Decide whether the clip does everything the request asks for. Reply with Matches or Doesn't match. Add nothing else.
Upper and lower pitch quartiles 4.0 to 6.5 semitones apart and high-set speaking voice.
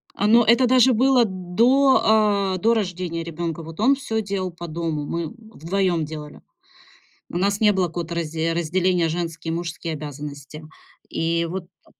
Doesn't match